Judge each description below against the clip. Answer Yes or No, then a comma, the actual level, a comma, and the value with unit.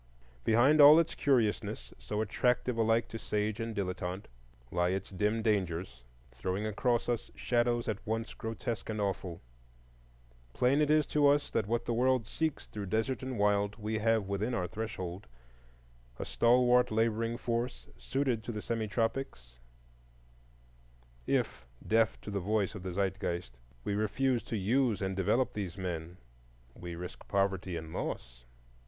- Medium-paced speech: Yes, average, 150 wpm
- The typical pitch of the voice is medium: No, low, 110 Hz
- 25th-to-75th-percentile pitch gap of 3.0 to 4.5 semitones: Yes, average, 4.1 semitones